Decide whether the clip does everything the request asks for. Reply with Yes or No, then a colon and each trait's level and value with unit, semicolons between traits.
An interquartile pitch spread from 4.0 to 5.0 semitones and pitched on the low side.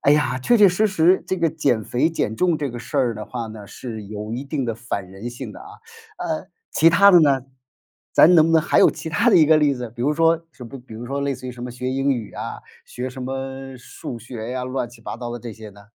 Yes: average, 4.6 semitones; low, 130 Hz